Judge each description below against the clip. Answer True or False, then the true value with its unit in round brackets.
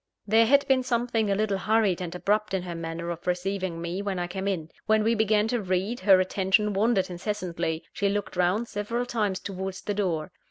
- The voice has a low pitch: False (195 Hz)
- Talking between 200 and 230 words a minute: True (205 wpm)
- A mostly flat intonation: False (3.2 semitones)